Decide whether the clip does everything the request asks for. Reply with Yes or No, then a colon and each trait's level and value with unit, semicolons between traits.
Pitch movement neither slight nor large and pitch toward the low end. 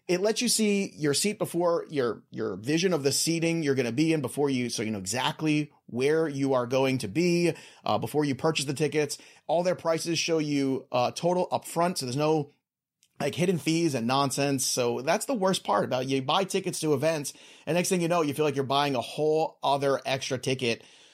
No: average, 3.8 semitones; medium, 150 Hz